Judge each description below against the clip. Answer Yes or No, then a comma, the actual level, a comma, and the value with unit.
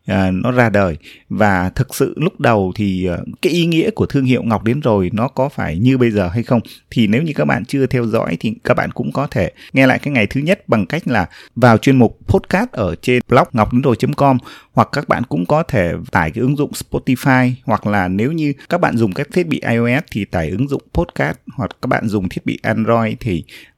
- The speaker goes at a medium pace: Yes, average, 235 wpm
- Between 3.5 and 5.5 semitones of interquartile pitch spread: Yes, average, 4.0 semitones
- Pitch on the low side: Yes, low, 125 Hz